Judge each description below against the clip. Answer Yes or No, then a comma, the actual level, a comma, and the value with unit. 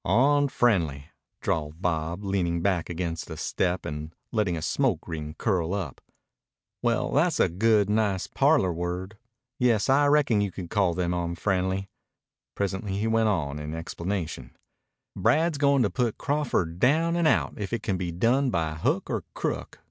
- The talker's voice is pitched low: Yes, very low, 95 Hz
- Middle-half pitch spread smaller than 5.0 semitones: No, wide, 5.6 semitones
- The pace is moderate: Yes, average, 160 wpm